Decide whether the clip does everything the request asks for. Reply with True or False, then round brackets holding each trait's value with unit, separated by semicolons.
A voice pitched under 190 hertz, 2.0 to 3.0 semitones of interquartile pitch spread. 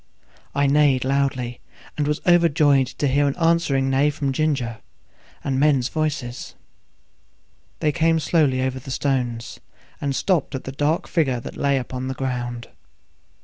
True (140 Hz; 2.6 semitones)